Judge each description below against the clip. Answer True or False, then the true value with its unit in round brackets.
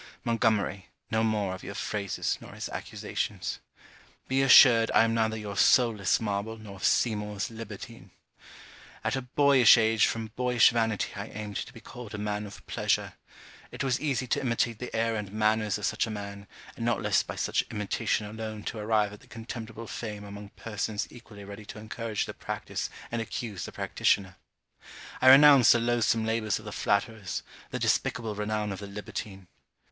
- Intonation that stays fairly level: True (1.9 semitones)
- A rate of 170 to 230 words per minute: True (180 wpm)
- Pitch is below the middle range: True (110 Hz)